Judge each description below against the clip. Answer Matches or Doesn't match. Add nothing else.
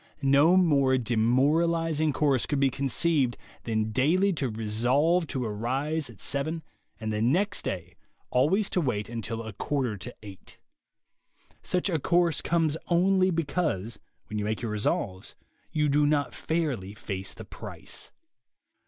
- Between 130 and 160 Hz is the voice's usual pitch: Matches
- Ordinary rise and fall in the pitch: Doesn't match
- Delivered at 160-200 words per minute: Doesn't match